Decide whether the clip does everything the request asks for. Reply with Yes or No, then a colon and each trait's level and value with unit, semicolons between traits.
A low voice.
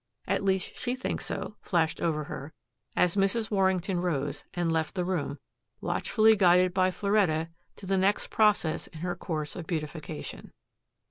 No: medium, 180 Hz